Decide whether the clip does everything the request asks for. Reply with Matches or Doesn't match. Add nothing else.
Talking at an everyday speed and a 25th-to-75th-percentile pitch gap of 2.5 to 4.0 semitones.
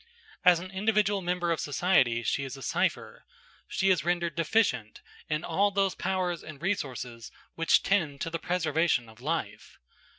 Doesn't match